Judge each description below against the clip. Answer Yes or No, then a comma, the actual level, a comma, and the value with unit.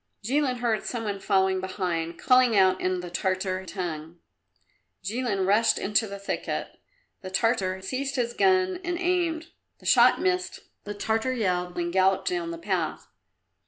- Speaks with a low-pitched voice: No, high, 205 Hz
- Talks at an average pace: Yes, average, 155 wpm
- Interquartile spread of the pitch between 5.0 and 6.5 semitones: Yes, wide, 5.6 semitones